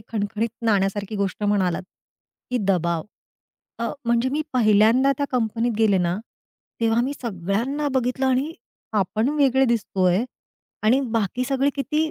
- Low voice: No, high, 230 Hz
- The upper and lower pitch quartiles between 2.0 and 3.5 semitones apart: No, average, 4.4 semitones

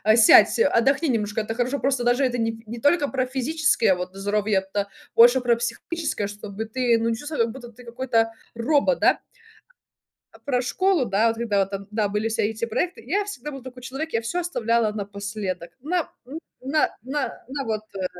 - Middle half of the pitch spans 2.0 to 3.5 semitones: No, average, 4.1 semitones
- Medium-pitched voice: No, high, 235 Hz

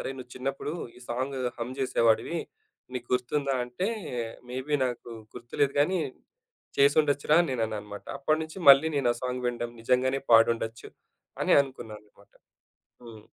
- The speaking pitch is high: No, low, 130 Hz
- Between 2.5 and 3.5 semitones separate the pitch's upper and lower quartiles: Yes, average, 2.9 semitones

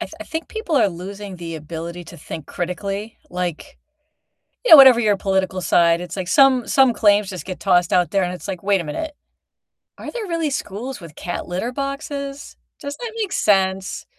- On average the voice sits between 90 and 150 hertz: No, high, 195 Hz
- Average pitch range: No, wide, 7.5 semitones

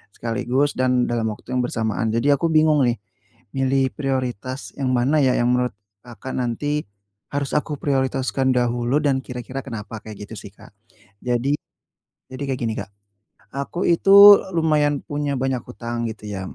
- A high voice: No, low, 130 Hz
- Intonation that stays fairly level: No, average, 3.1 semitones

